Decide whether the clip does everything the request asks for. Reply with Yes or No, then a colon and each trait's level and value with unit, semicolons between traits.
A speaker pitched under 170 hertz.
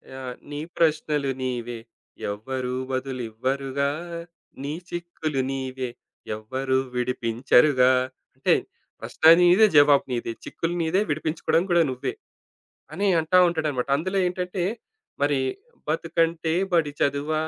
Yes: medium, 140 Hz